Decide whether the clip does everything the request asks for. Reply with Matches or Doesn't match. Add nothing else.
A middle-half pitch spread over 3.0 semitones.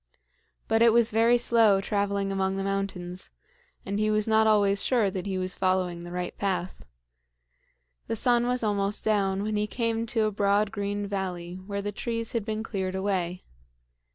Doesn't match